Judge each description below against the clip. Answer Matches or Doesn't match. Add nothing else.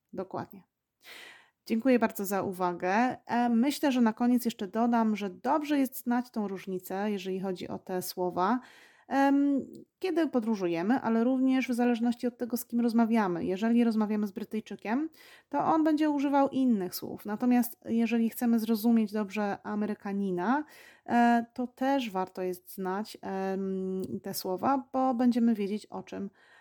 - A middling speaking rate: Matches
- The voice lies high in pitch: Matches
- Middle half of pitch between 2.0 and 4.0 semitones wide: Doesn't match